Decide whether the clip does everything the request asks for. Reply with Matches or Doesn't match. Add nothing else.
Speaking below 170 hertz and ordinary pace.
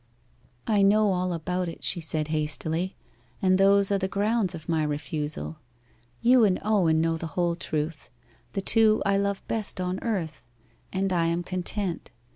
Doesn't match